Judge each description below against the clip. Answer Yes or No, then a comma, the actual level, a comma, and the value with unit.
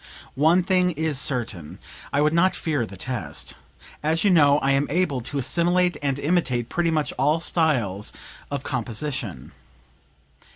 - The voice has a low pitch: No, medium, 145 Hz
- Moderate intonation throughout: Yes, average, 4.9 semitones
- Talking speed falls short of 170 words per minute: Yes, average, 150 wpm